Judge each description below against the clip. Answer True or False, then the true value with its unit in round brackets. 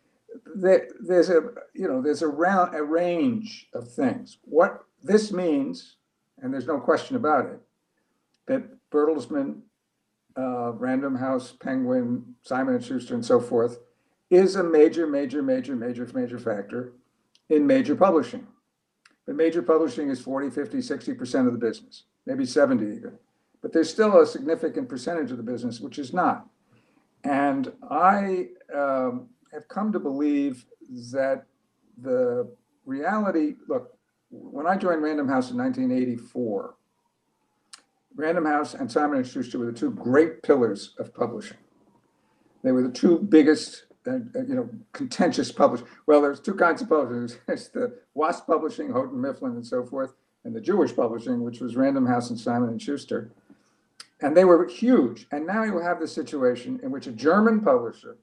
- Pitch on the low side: False (185 Hz)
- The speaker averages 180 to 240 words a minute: False (155 wpm)